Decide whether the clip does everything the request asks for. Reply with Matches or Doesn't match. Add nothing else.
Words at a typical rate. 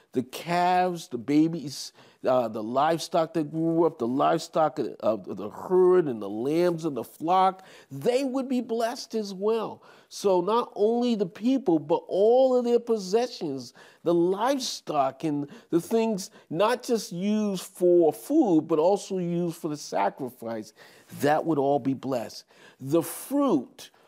Matches